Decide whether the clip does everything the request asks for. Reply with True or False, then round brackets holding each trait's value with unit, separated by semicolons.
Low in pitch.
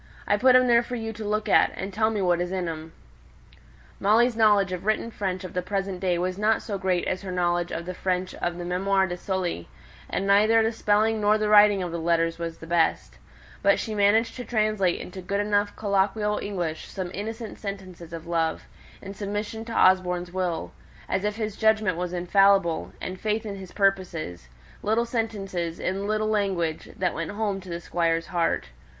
False (195 Hz)